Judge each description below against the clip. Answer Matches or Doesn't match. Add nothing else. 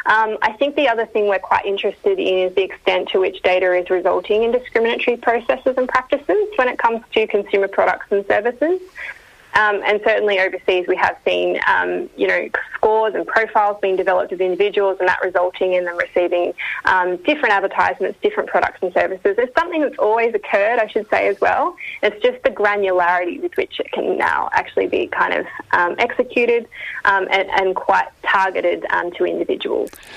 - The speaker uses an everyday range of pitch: Doesn't match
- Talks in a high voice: Matches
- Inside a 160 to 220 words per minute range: Matches